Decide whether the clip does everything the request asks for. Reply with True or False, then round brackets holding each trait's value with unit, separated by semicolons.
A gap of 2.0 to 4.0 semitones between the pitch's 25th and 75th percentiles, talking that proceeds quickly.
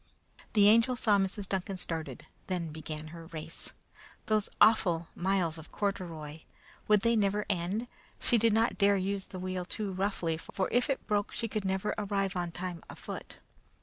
False (3.5 semitones; 170 wpm)